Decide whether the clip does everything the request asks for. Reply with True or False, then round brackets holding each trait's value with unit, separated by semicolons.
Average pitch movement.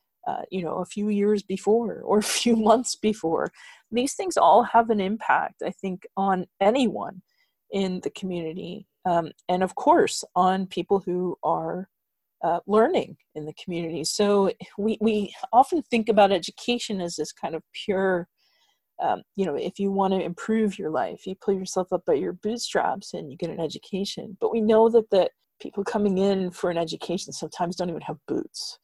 True (3.4 semitones)